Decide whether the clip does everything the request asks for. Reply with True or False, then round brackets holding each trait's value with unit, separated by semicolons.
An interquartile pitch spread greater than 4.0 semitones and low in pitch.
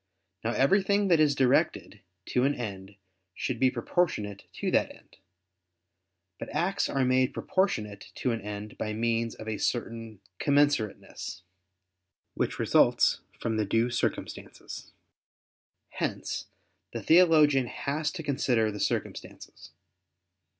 True (5.1 semitones; 125 Hz)